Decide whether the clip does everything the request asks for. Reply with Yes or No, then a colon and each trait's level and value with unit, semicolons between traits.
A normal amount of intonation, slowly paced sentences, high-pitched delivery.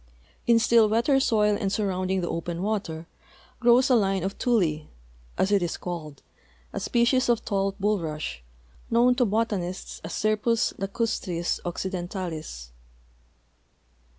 Yes: average, 4.7 semitones; slow, 125 wpm; high, 195 Hz